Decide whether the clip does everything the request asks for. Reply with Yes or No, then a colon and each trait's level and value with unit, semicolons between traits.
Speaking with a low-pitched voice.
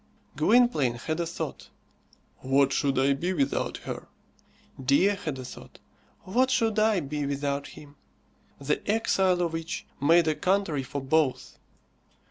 No: medium, 155 Hz